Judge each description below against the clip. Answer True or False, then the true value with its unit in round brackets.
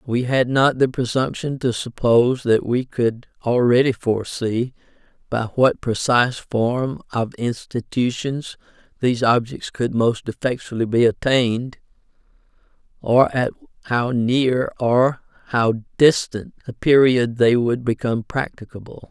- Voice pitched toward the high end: False (120 Hz)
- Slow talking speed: True (120 wpm)